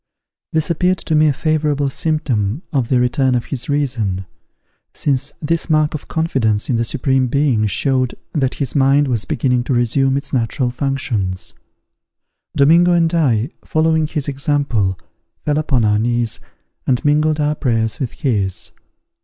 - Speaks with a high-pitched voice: No, low, 135 Hz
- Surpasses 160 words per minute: No, average, 155 wpm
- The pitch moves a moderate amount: Yes, average, 4.1 semitones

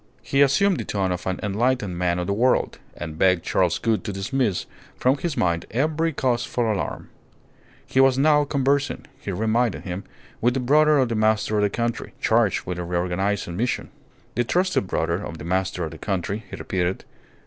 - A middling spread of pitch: No, wide, 6.1 semitones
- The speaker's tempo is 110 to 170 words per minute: No, average, 190 wpm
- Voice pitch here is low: Yes, low, 110 Hz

